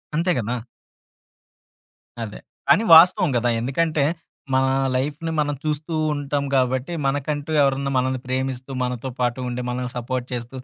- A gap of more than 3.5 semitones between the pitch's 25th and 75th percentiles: No, average, 2.9 semitones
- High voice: No, low, 135 Hz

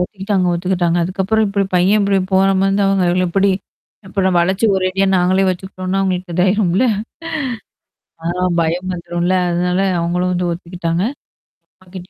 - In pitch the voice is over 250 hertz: No, medium, 185 Hz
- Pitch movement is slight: Yes, narrow, 1.6 semitones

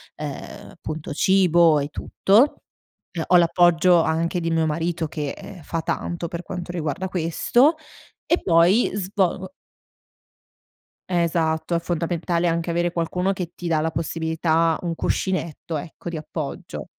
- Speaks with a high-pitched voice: No, medium, 170 Hz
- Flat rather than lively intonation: Yes, narrow, 1.7 semitones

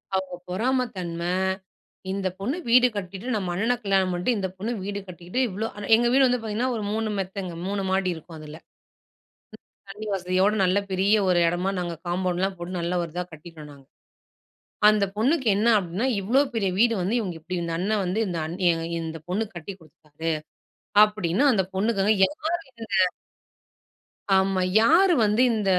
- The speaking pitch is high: Yes, high, 195 Hz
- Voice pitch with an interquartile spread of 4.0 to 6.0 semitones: No, average, 3.6 semitones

